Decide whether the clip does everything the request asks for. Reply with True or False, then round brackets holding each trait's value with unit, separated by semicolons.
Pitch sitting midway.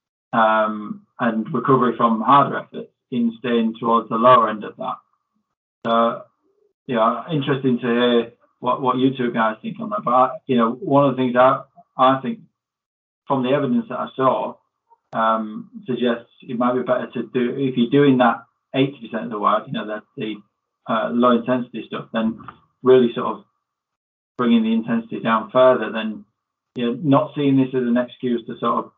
False (125 Hz)